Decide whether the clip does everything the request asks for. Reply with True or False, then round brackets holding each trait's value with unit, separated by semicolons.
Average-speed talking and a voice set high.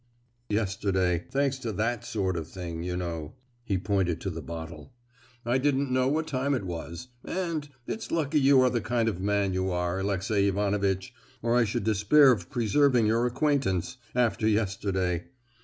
False (165 wpm; 105 Hz)